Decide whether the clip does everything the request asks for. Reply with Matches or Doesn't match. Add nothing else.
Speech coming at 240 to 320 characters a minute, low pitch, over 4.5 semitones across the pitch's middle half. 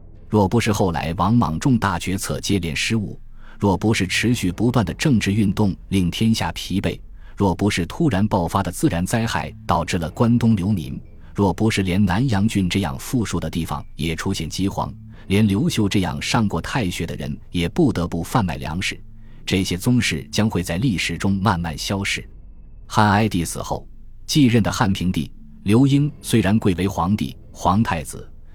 Doesn't match